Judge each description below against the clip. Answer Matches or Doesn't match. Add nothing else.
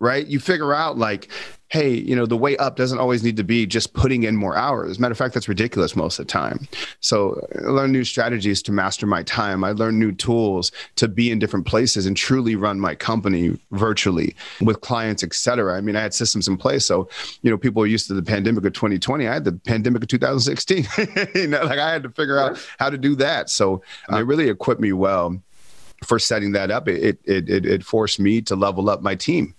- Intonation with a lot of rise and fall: Doesn't match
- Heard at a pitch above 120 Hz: Doesn't match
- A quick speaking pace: Matches